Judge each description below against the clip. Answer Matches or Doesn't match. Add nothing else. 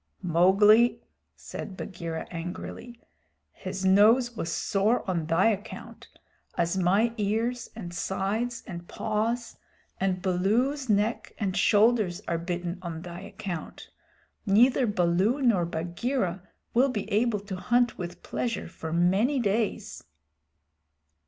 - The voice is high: Matches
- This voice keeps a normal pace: Doesn't match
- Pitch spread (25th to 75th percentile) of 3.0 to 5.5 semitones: Matches